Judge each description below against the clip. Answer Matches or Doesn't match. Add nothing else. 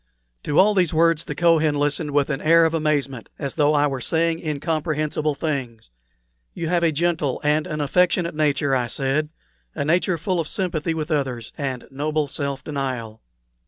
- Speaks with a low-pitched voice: Doesn't match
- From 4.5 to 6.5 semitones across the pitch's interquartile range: Doesn't match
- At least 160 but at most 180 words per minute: Matches